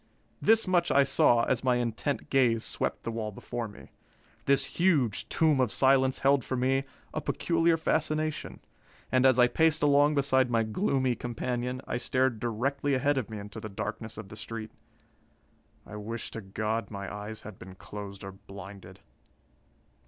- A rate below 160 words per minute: No, average, 165 wpm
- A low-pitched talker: Yes, low, 125 Hz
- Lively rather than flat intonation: No, average, 4.3 semitones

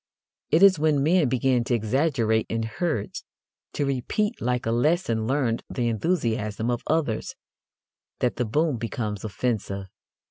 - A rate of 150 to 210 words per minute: No, average, 140 wpm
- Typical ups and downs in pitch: Yes, average, 4.9 semitones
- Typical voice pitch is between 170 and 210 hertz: No, low, 125 Hz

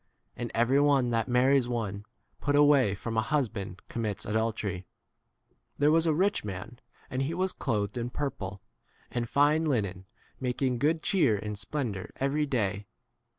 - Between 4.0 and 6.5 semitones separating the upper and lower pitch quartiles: Yes, wide, 5.5 semitones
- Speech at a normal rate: Yes, average, 165 wpm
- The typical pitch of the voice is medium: No, low, 120 Hz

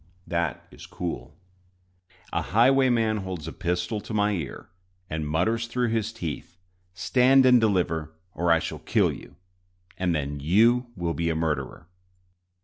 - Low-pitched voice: Yes, very low, 90 Hz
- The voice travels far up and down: Yes, wide, 6.0 semitones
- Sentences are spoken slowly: No, average, 145 wpm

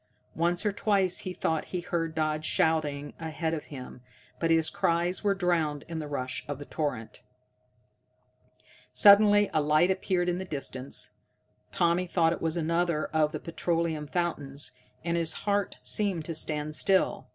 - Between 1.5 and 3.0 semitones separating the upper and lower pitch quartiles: Yes, average, 2.7 semitones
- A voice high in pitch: No, medium, 165 Hz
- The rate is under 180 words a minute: Yes, average, 160 wpm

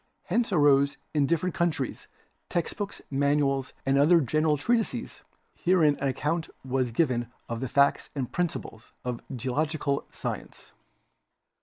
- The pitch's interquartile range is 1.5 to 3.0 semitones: No, average, 3.9 semitones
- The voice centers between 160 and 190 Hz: No, medium, 145 Hz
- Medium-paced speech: No, slow, 130 wpm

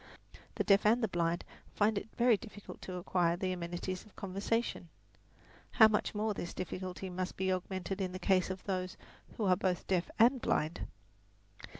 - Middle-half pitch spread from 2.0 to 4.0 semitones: Yes, narrow, 2.5 semitones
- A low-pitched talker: No, medium, 185 Hz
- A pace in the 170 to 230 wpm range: Yes, average, 175 wpm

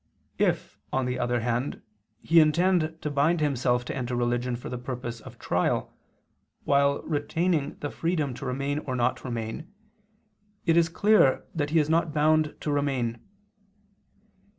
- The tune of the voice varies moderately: Yes, average, 4.2 semitones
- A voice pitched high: No, medium, 140 Hz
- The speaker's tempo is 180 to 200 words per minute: No, average, 150 wpm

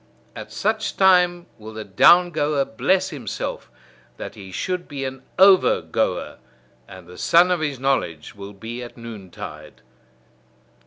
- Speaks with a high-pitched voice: No, low, 135 Hz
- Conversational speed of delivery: Yes, average, 145 wpm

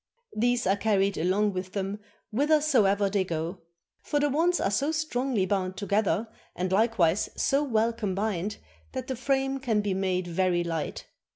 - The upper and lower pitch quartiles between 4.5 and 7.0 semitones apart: Yes, average, 5.2 semitones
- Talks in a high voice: Yes, high, 205 Hz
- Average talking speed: Yes, average, 160 wpm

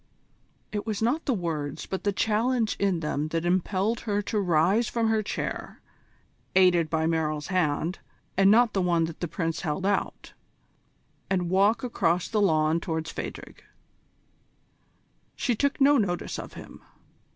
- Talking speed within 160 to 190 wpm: No, average, 150 wpm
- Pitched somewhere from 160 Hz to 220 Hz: Yes, medium, 185 Hz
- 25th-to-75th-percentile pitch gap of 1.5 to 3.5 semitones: No, average, 4.7 semitones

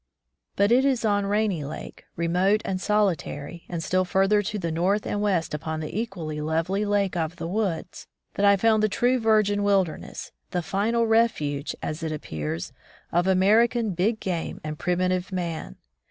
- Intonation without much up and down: No, average, 4.2 semitones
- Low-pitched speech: No, high, 190 Hz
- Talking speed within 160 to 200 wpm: Yes, average, 170 wpm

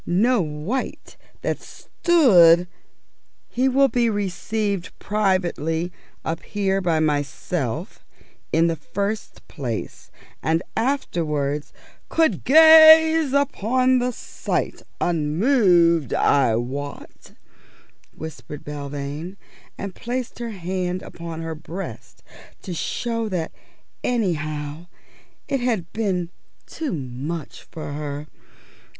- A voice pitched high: No, medium, 180 Hz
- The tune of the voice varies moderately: No, wide, 7.0 semitones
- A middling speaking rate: No, slow, 100 wpm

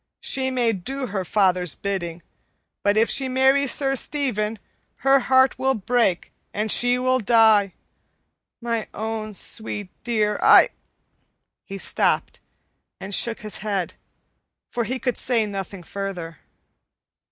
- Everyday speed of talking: No, slow, 130 wpm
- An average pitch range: Yes, average, 4.3 semitones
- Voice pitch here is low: No, high, 220 Hz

